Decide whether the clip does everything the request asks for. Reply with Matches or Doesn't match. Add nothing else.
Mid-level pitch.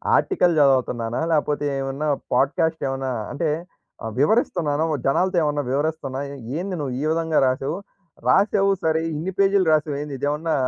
Matches